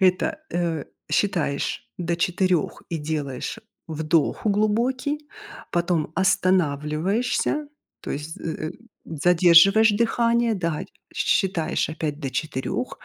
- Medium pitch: Yes, medium, 175 Hz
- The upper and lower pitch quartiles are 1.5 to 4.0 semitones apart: No, average, 4.7 semitones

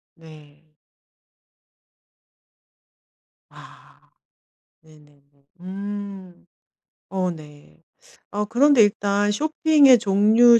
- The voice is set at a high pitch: Yes, high, 200 Hz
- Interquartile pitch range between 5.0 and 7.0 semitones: Yes, wide, 5.6 semitones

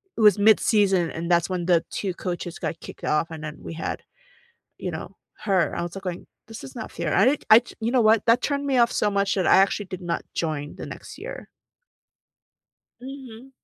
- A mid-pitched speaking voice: No, high, 195 Hz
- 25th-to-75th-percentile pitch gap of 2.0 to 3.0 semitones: No, average, 4.6 semitones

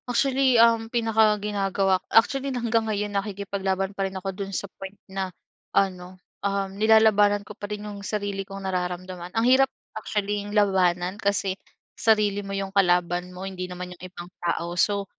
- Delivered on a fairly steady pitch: Yes, narrow, 2.0 semitones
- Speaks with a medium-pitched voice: No, high, 200 Hz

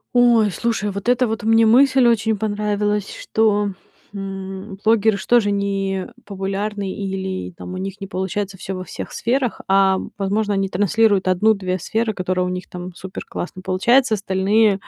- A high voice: Yes, high, 200 Hz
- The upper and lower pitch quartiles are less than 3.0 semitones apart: Yes, narrow, 2.4 semitones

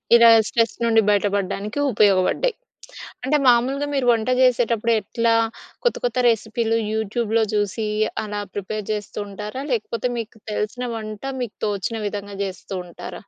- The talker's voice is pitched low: No, high, 220 Hz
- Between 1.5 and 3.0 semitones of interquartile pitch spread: Yes, narrow, 2.4 semitones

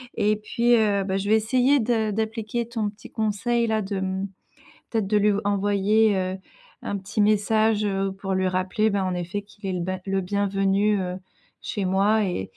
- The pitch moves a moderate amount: No, narrow, 2.1 semitones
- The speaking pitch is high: Yes, high, 205 Hz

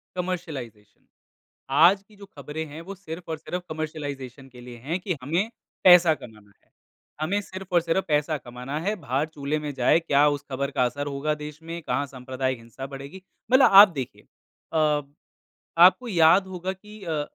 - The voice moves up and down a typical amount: Yes, average, 4.5 semitones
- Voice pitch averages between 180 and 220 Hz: No, medium, 155 Hz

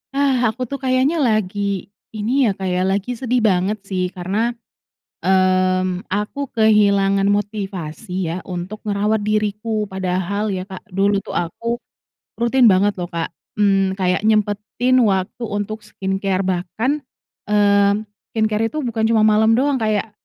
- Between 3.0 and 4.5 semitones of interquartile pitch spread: No, narrow, 2.6 semitones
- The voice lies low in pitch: No, high, 205 Hz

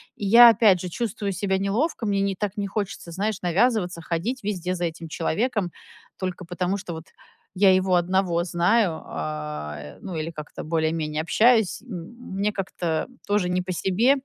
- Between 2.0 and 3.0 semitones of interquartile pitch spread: No, average, 3.6 semitones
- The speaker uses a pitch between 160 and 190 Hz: Yes, medium, 185 Hz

